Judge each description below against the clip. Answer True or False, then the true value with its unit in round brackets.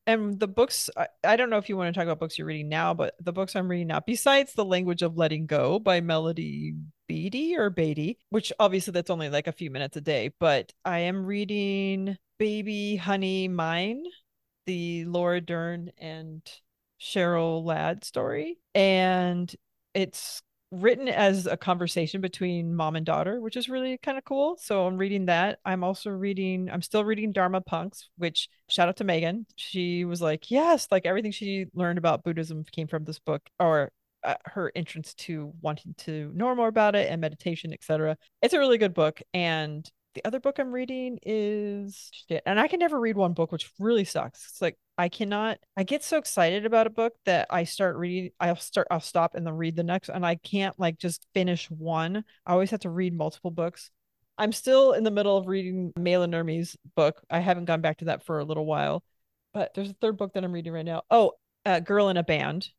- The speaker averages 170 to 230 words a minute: True (205 wpm)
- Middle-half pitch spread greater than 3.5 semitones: True (3.9 semitones)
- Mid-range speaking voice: True (180 Hz)